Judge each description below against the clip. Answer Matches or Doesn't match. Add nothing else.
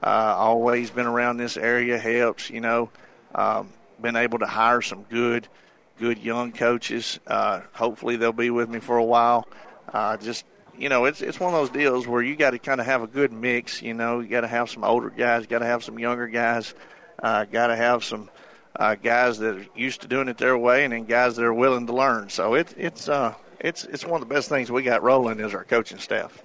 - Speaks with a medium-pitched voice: Doesn't match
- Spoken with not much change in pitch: Matches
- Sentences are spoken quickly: Matches